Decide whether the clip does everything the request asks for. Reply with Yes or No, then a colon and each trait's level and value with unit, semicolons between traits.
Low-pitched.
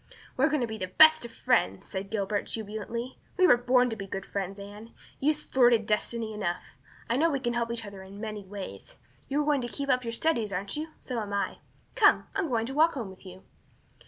No: high, 230 Hz